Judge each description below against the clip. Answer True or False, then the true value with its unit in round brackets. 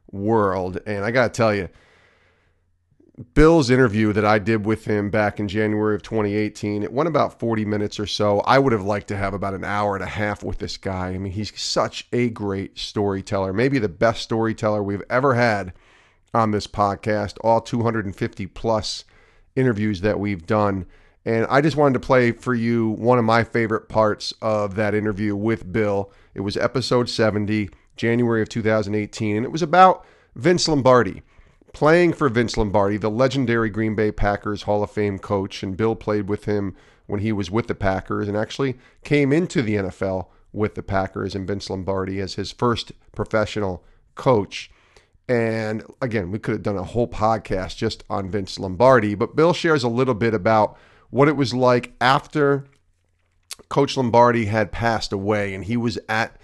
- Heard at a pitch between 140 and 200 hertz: False (110 Hz)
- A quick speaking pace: False (180 wpm)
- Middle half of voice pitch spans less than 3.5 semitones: True (2.7 semitones)